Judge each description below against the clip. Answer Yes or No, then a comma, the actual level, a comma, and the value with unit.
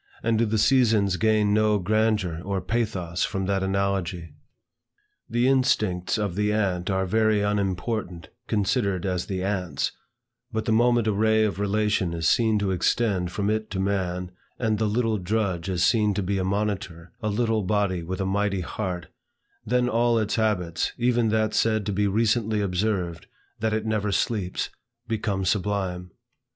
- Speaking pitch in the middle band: No, low, 105 Hz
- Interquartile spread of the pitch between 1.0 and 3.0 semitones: Yes, average, 2.7 semitones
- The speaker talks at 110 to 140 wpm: No, average, 165 wpm